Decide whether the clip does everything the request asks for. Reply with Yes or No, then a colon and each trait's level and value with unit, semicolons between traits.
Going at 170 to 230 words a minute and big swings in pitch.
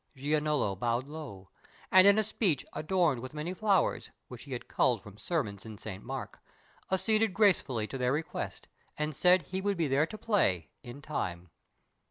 Yes: average, 175 wpm; wide, 7.5 semitones